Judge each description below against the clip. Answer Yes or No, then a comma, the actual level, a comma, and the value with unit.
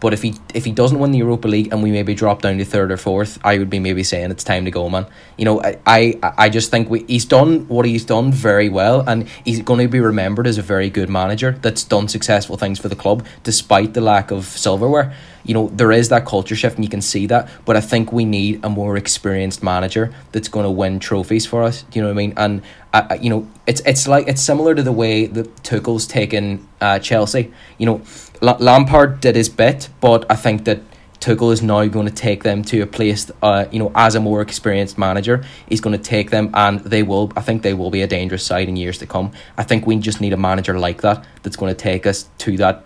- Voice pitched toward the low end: Yes, low, 110 Hz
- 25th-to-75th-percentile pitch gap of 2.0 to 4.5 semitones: Yes, narrow, 2.4 semitones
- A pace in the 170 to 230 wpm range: No, fast, 255 wpm